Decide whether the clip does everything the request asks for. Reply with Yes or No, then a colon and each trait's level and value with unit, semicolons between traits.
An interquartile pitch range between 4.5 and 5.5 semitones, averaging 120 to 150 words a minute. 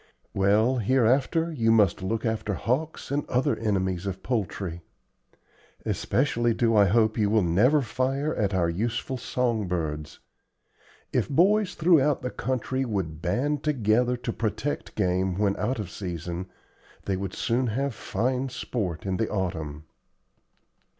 Yes: average, 5.2 semitones; average, 140 wpm